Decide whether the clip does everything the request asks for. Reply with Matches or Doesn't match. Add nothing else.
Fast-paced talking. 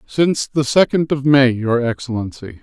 Doesn't match